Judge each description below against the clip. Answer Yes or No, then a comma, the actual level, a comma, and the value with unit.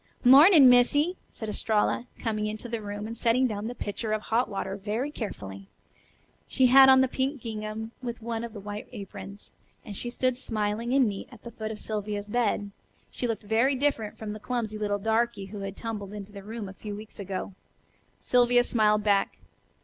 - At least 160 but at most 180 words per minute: No, average, 195 wpm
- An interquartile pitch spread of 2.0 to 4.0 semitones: Yes, average, 2.8 semitones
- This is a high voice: Yes, high, 220 Hz